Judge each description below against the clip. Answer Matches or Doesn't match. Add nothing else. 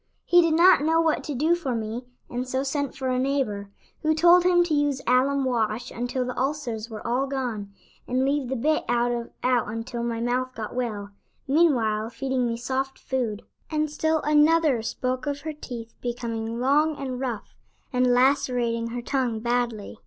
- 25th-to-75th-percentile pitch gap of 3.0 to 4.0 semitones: Matches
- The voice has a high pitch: Matches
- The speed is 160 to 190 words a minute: Matches